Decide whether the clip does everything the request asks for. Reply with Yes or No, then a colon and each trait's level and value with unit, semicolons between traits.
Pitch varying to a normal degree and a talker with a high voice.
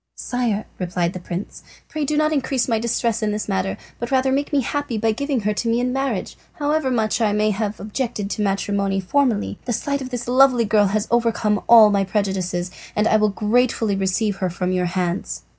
Yes: average, 4.0 semitones; high, 215 Hz